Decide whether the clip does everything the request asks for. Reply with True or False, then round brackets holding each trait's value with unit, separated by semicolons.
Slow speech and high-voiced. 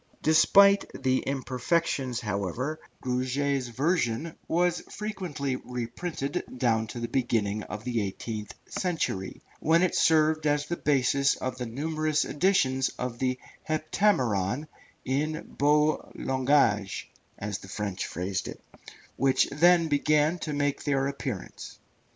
False (120 wpm; 135 Hz)